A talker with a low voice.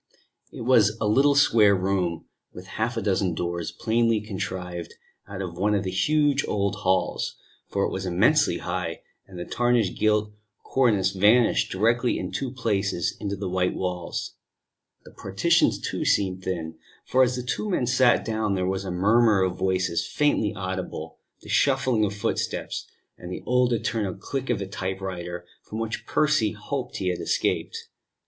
Yes: low, 100 Hz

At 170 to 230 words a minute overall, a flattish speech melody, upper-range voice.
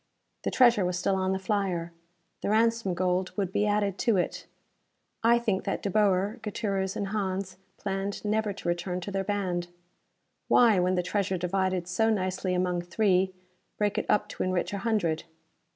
Yes: average, 175 wpm; narrow, 2.3 semitones; high, 195 Hz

